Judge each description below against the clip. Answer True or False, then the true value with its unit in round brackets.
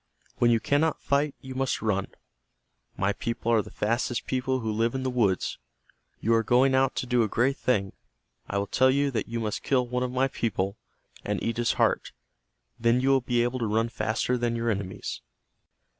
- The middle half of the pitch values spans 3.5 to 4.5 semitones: False (2.6 semitones)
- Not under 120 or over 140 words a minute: False (205 wpm)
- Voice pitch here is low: True (120 Hz)